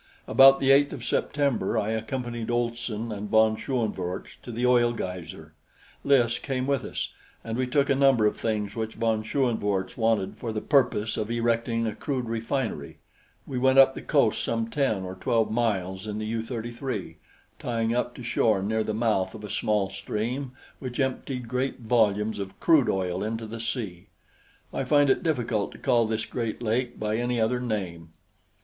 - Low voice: Yes, low, 115 Hz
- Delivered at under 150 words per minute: No, average, 180 wpm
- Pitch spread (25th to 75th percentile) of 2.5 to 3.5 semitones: Yes, average, 2.8 semitones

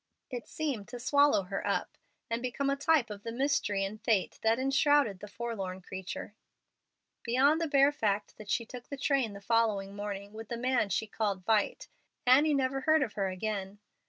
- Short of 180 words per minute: No, average, 190 wpm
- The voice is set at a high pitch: Yes, high, 230 Hz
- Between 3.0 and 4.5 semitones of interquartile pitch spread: No, average, 5.1 semitones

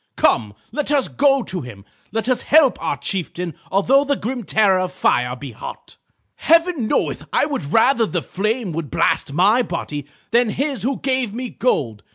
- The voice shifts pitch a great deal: Yes, wide, 7.6 semitones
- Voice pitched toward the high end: Yes, high, 220 Hz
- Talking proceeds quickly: No, average, 180 wpm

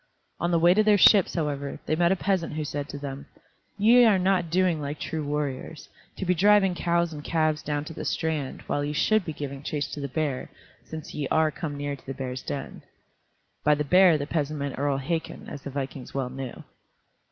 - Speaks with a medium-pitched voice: Yes, medium, 150 Hz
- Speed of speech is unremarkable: No, fast, 220 wpm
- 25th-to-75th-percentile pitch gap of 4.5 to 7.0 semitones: No, average, 3.4 semitones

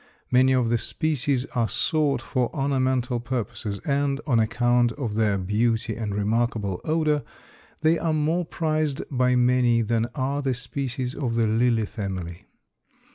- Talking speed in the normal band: Yes, average, 145 wpm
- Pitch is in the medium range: No, low, 125 Hz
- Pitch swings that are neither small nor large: Yes, average, 3.5 semitones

